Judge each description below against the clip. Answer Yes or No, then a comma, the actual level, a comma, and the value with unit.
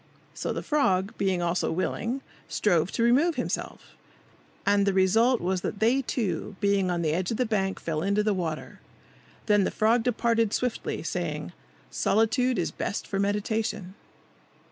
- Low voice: No, high, 205 Hz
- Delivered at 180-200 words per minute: No, average, 160 wpm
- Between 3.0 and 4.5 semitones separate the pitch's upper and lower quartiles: Yes, average, 3.6 semitones